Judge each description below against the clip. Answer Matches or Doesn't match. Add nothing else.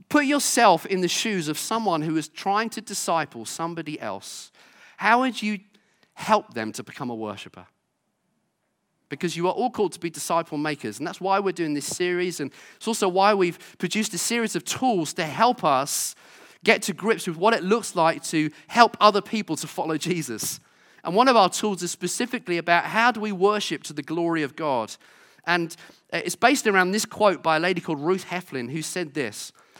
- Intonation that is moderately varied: Matches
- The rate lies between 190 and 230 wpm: Matches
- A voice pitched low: Doesn't match